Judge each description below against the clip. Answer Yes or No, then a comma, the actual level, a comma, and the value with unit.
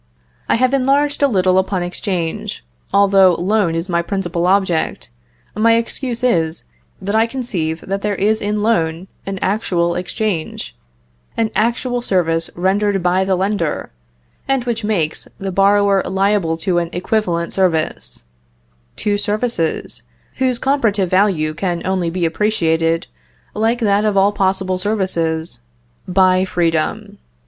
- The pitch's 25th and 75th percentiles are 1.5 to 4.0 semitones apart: Yes, average, 3.7 semitones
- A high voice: Yes, high, 195 Hz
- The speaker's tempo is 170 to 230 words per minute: No, slow, 135 wpm